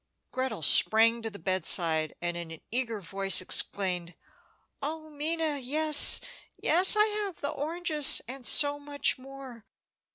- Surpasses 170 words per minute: No, slow, 135 wpm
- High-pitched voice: Yes, very high, 260 Hz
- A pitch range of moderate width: No, wide, 7.6 semitones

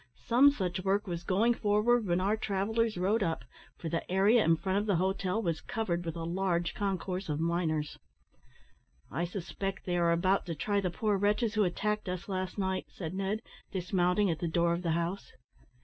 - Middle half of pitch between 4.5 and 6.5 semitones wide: No, average, 3.1 semitones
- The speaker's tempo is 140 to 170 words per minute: No, average, 195 wpm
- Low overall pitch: No, high, 190 Hz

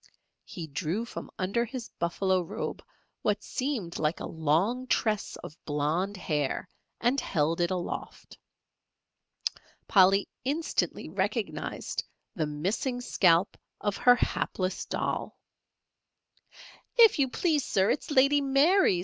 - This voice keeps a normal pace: No, slow, 115 wpm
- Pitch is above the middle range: Yes, high, 195 Hz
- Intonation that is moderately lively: No, wide, 7.0 semitones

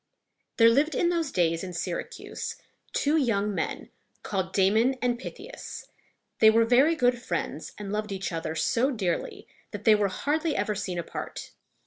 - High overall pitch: Yes, high, 220 Hz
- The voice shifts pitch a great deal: Yes, wide, 5.7 semitones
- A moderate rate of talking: Yes, average, 165 wpm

